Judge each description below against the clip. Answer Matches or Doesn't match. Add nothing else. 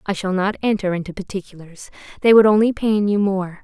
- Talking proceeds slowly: Doesn't match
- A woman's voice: Matches